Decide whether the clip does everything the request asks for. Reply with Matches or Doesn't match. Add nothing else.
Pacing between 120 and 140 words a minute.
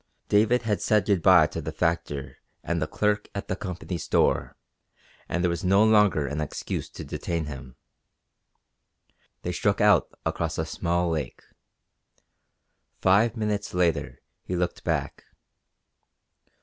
Matches